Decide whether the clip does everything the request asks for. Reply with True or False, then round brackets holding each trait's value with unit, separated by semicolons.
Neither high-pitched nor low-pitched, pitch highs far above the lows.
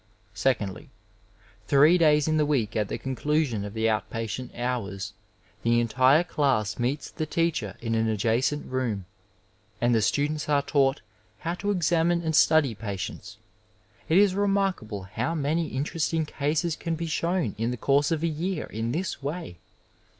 True (145 Hz; 6.1 semitones)